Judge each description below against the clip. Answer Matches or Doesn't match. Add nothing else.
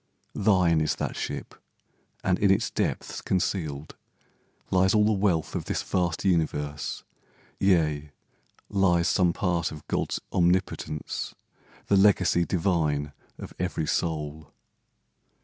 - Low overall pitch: Matches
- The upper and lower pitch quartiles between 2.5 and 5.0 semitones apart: Matches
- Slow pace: Matches